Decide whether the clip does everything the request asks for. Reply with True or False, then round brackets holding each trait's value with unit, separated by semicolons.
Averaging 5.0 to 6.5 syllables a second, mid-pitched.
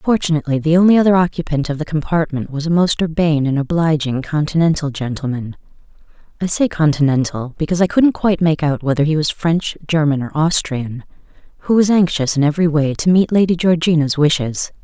True (5.9 syllables/s; 155 Hz)